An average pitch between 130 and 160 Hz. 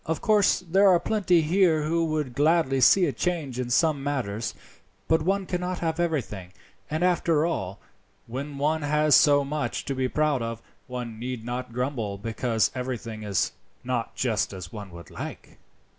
Yes: medium, 140 Hz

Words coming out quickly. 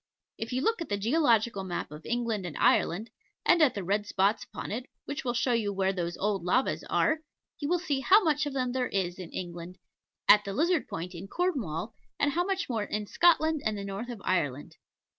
Yes: fast, 215 wpm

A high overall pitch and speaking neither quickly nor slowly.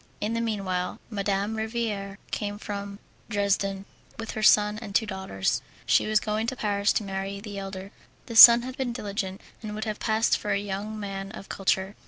Yes: high, 205 Hz; average, 190 wpm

